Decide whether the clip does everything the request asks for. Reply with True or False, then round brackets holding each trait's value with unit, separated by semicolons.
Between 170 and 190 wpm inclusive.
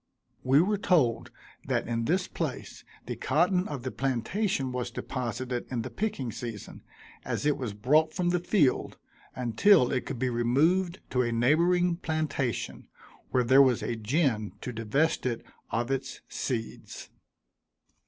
False (150 wpm)